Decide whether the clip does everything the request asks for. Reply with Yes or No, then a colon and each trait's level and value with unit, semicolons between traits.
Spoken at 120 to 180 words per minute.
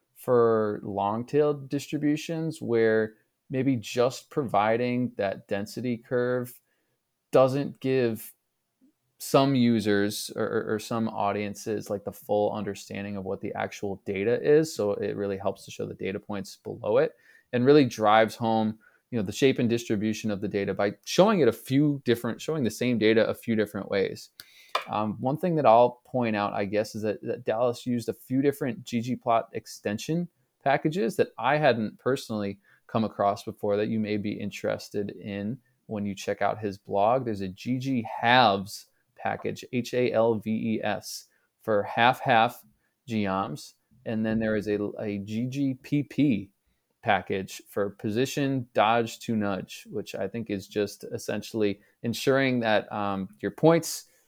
Yes: average, 155 wpm